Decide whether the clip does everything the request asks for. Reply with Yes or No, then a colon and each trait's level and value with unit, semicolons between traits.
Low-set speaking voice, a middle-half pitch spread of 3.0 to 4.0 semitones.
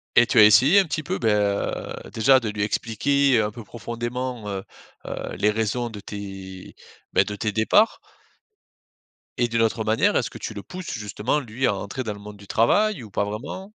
Yes: low, 110 Hz; average, 3.6 semitones